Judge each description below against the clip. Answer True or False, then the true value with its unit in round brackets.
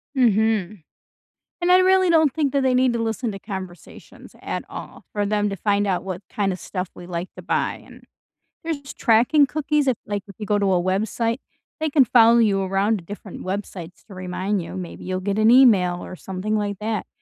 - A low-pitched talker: False (210 Hz)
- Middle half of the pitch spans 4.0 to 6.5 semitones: True (4.6 semitones)